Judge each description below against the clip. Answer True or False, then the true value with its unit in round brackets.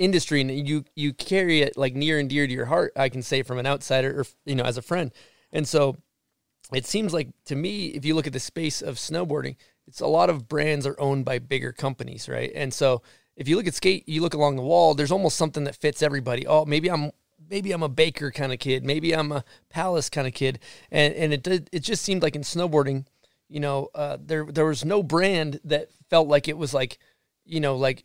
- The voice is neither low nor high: True (150 Hz)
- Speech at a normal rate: False (240 wpm)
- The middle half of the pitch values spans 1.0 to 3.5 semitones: True (2.8 semitones)